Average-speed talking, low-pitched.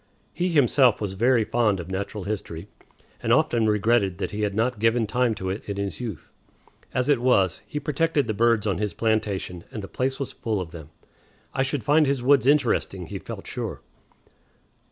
Yes: average, 195 wpm; low, 110 Hz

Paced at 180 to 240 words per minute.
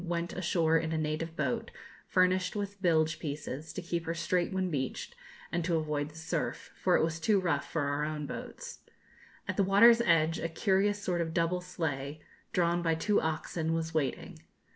Yes: average, 185 wpm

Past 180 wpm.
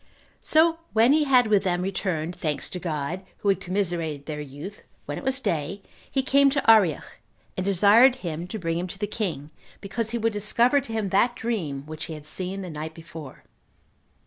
Yes: average, 200 wpm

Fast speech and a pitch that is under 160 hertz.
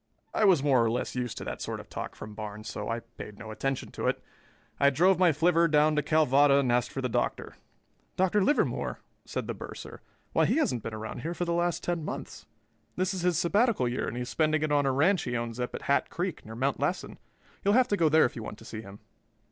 Yes: fast, 250 wpm; medium, 140 Hz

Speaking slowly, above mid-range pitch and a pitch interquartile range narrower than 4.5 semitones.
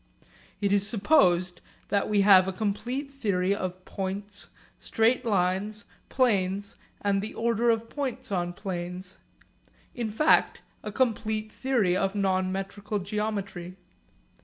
Yes: slow, 125 wpm; high, 200 Hz; average, 2.9 semitones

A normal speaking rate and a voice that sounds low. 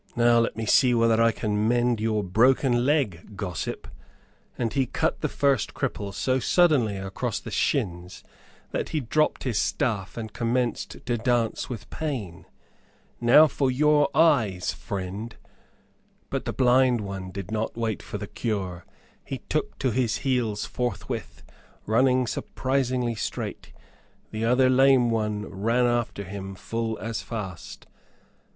Yes: average, 145 wpm; low, 115 Hz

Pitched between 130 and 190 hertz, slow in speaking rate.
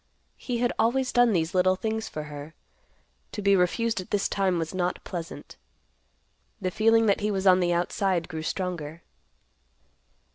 No: medium, 185 Hz; average, 160 wpm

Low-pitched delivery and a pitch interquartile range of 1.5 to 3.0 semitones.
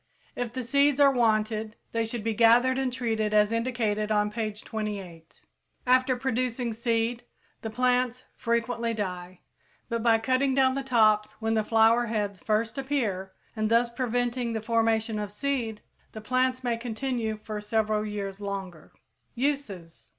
No: high, 225 Hz; average, 2.7 semitones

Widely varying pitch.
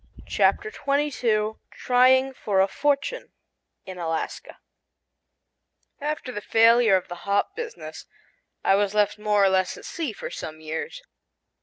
Yes: wide, 6.2 semitones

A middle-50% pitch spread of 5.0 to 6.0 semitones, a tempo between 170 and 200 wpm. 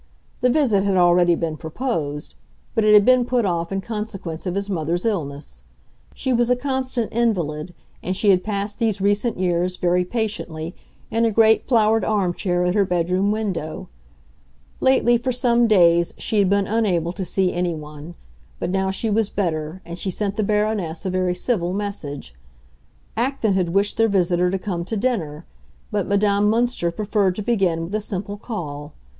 No: average, 4.0 semitones; average, 175 wpm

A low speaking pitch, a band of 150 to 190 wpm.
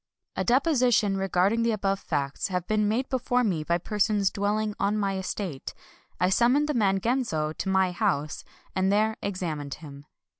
No: high, 200 Hz; average, 175 wpm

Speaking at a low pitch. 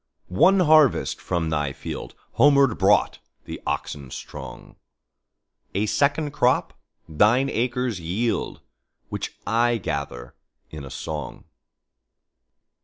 Yes: low, 110 Hz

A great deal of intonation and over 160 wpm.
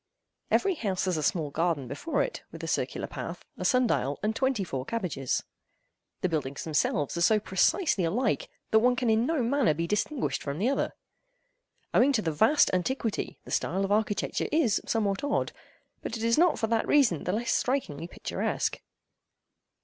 Yes: wide, 7.2 semitones; average, 180 wpm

